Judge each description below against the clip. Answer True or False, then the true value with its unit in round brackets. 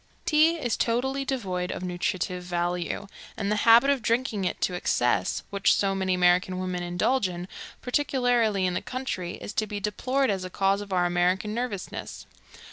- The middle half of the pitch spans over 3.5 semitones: True (5.1 semitones)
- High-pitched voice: True (195 Hz)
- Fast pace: False (175 wpm)